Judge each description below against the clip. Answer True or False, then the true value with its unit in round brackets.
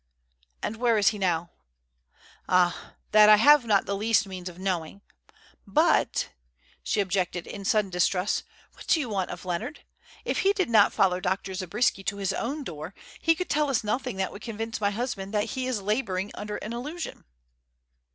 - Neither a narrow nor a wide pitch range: True (3.9 semitones)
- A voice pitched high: True (205 Hz)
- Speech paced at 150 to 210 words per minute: True (180 wpm)